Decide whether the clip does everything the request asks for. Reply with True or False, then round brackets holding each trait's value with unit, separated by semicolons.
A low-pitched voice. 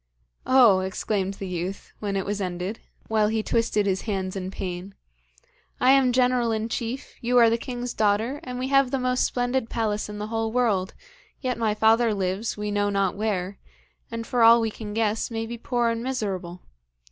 False (220 Hz)